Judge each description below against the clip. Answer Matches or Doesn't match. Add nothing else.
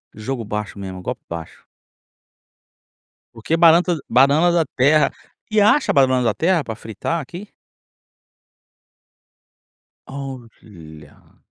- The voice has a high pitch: Doesn't match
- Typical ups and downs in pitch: Doesn't match